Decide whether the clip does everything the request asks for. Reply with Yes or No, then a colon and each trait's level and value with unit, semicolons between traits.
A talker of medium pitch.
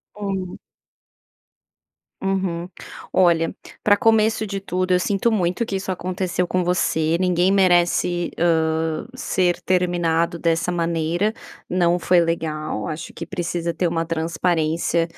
Yes: medium, 175 Hz